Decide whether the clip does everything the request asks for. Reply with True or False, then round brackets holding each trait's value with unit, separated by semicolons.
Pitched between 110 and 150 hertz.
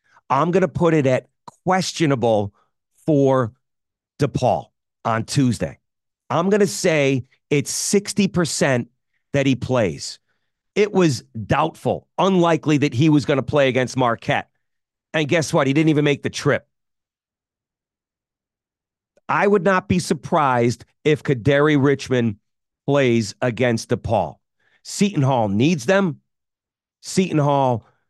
True (140 Hz)